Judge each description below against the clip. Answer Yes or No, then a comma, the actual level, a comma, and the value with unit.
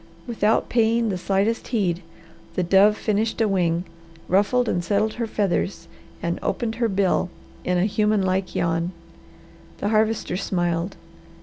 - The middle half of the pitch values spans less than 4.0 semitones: Yes, average, 3.4 semitones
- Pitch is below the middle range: No, high, 200 Hz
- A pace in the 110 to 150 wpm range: Yes, average, 140 wpm